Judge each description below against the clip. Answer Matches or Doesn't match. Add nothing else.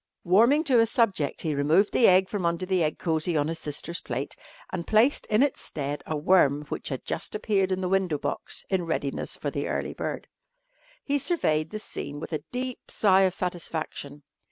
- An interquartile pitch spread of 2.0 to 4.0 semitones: Doesn't match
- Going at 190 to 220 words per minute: Matches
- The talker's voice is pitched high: Doesn't match